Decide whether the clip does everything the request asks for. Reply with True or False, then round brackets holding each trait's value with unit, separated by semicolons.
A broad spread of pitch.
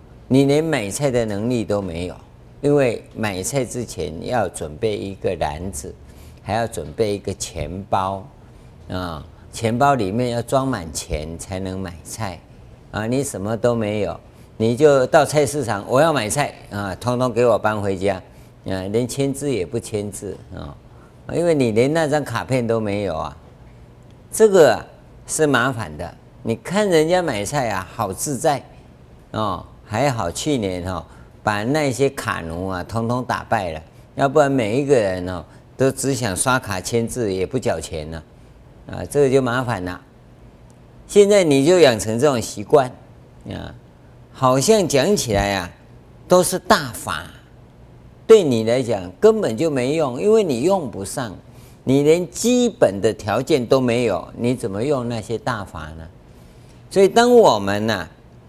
True (5.9 semitones)